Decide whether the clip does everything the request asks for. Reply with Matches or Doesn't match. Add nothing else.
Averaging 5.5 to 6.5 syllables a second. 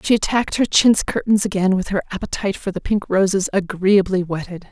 Matches